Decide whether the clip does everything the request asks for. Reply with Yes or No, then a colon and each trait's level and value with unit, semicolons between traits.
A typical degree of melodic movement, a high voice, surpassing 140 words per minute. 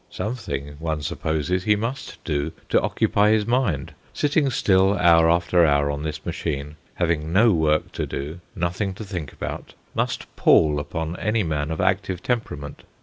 No: average, 5.0 semitones; very low, 85 Hz; average, 160 wpm